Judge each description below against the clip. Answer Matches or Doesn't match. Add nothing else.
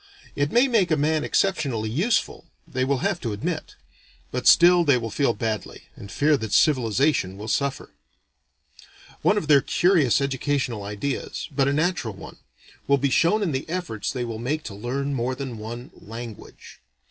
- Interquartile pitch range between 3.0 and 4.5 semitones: Doesn't match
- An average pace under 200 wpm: Matches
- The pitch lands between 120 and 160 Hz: Matches